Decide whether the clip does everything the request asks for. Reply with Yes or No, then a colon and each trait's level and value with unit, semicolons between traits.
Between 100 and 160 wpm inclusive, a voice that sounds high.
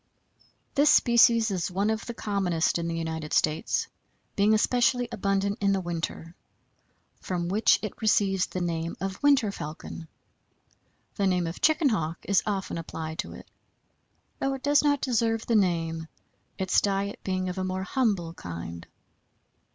Yes: average, 155 wpm; high, 195 Hz